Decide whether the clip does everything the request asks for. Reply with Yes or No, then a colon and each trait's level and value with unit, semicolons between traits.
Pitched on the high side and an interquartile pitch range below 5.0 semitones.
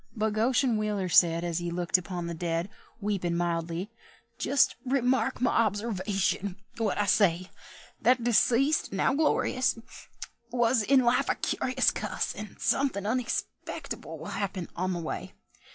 No: high, 210 Hz; wide, 5.4 semitones